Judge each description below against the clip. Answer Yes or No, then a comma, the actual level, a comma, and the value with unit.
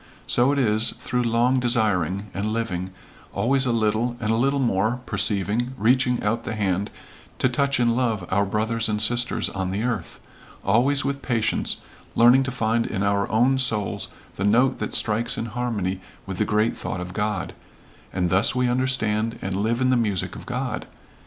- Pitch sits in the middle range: No, low, 115 Hz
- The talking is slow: No, average, 180 wpm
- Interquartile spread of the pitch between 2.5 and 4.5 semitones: Yes, average, 3.4 semitones